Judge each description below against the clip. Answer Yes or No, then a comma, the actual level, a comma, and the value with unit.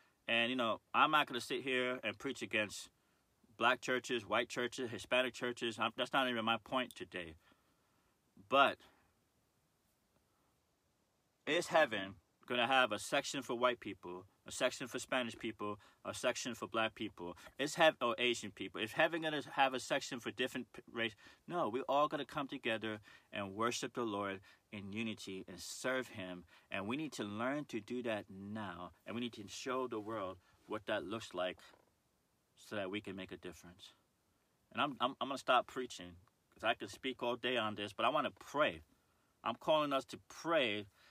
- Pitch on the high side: No, low, 115 Hz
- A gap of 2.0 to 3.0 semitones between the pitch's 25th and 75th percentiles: No, average, 3.7 semitones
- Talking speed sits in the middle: Yes, average, 190 wpm